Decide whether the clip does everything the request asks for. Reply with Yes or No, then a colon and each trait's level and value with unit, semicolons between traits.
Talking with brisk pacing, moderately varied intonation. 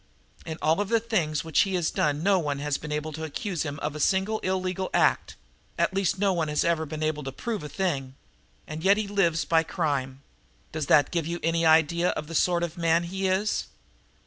Yes: fast, 225 wpm; average, 3.7 semitones